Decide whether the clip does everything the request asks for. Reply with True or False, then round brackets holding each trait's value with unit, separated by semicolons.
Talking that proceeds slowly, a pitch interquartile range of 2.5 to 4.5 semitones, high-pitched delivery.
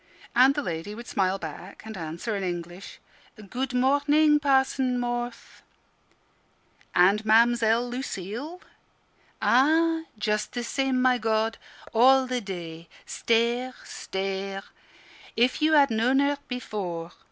False (120 wpm; 5.2 semitones; 235 Hz)